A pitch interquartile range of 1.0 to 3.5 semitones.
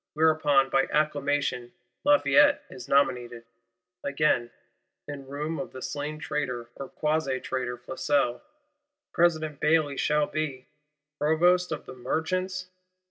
Yes: average, 2.8 semitones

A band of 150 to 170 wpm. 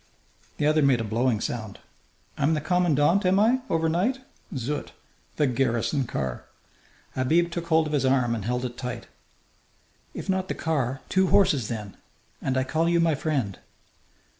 Yes: average, 165 wpm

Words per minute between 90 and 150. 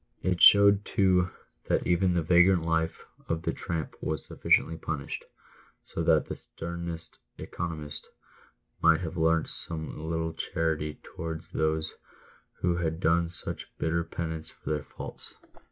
Yes: average, 140 wpm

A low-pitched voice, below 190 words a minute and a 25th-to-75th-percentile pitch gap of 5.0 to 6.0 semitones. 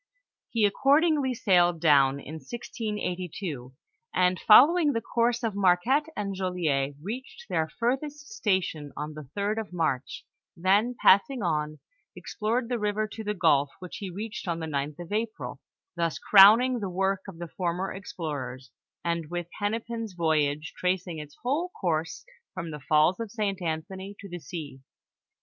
No: medium, 185 Hz; average, 155 wpm; wide, 5.6 semitones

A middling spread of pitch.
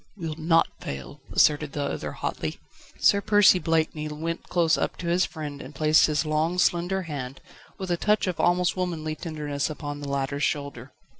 Yes: average, 3.2 semitones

